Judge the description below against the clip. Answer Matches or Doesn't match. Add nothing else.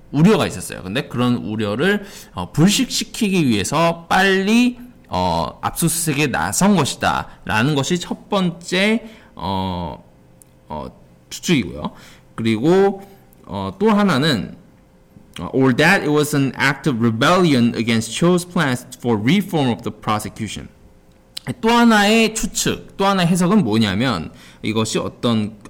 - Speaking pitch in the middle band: Matches